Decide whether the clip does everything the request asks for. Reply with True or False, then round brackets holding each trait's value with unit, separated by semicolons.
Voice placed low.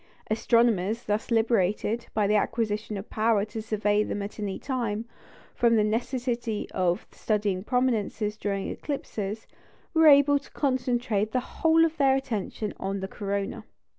False (220 Hz)